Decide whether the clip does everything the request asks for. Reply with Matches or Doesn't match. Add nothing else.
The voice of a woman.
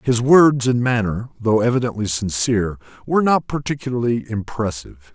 Doesn't match